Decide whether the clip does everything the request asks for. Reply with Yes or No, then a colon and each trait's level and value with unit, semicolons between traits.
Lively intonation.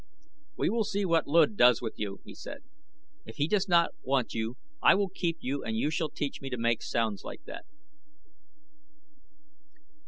Yes: wide, 7.2 semitones